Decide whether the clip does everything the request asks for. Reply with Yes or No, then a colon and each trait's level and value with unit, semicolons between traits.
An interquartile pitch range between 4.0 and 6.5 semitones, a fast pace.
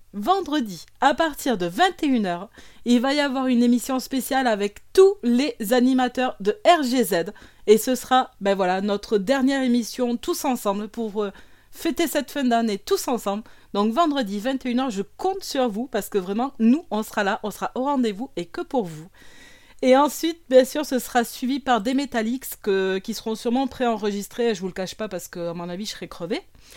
No: average, 4.3 semitones; average, 195 wpm